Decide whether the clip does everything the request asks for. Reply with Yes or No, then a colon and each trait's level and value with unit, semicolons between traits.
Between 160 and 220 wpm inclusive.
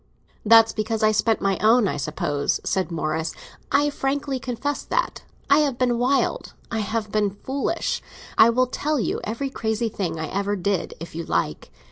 Yes: average, 175 wpm